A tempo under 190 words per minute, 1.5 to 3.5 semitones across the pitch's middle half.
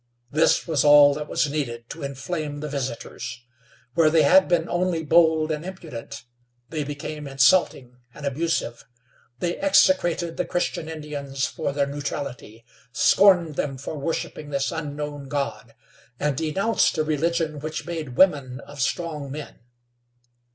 Yes: average, 140 wpm; average, 2.8 semitones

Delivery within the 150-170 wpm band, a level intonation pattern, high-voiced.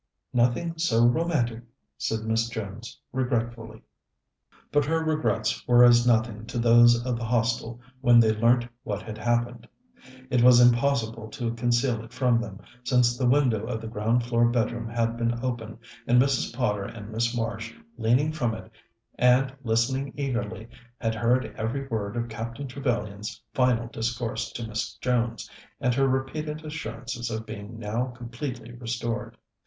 No: average, 155 wpm; narrow, 1.8 semitones; low, 120 Hz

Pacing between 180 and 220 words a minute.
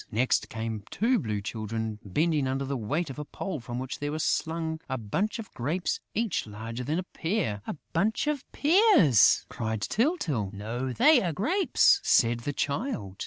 No: average, 170 wpm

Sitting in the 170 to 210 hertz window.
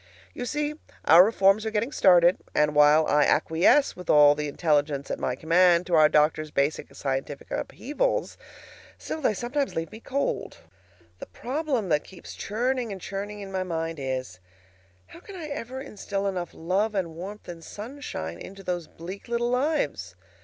Yes: medium, 185 Hz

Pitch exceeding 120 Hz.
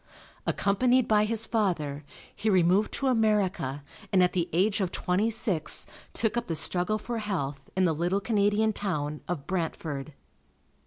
Yes: high, 190 Hz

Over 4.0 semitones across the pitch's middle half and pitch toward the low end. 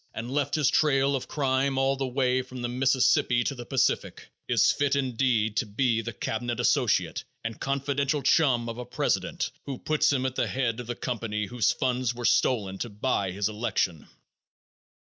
No: average, 2.7 semitones; low, 125 Hz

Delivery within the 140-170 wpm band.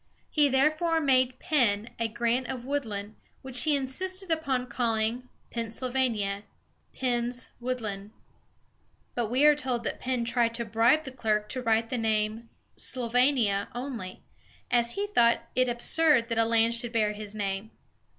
Yes: average, 160 wpm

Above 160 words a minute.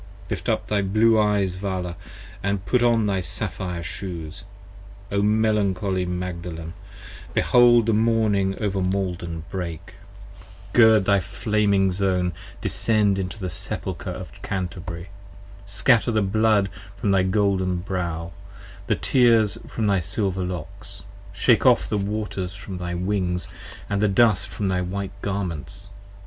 No: average, 140 wpm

